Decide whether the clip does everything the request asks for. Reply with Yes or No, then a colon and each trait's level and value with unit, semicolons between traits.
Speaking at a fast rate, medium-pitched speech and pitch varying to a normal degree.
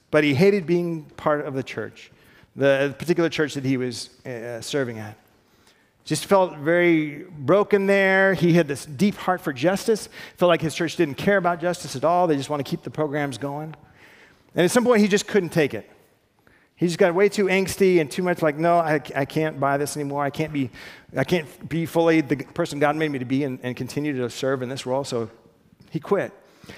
Yes: fast, 215 wpm; medium, 155 Hz; average, 4.3 semitones